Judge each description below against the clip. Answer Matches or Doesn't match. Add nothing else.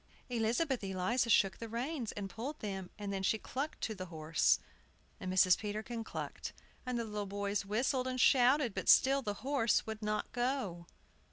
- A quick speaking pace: Doesn't match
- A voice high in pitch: Matches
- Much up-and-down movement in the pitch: Doesn't match